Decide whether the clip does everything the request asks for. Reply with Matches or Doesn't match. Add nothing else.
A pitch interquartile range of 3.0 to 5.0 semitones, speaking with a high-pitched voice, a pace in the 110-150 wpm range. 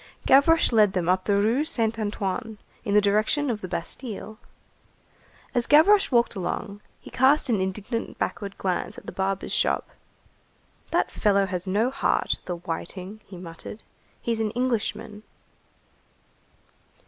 Matches